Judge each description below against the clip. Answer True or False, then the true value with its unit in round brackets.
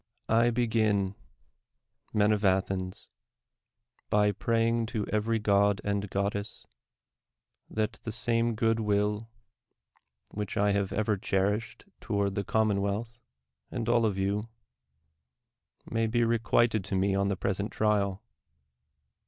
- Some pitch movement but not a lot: False (2.2 semitones)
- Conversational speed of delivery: False (120 wpm)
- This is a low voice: True (105 Hz)